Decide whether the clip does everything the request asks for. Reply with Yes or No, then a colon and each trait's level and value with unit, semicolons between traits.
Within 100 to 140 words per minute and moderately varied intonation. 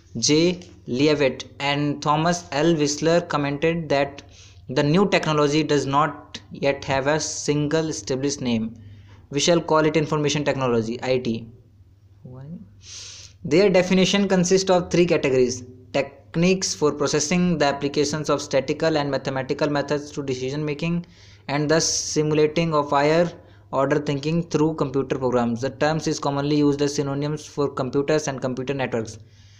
Yes: slow, 135 wpm; average, 3.1 semitones